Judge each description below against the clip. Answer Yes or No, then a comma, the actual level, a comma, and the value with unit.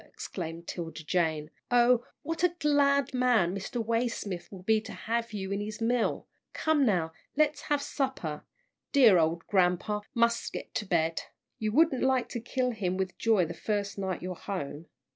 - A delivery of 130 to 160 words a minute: No, average, 170 wpm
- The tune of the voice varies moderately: No, wide, 5.8 semitones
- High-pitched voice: Yes, high, 215 Hz